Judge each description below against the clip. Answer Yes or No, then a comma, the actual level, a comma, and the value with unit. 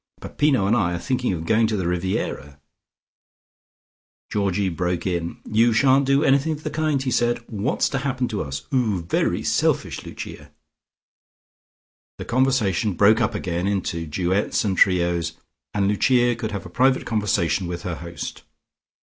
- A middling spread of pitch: No, wide, 6.0 semitones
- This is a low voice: Yes, low, 105 Hz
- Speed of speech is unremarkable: Yes, average, 160 wpm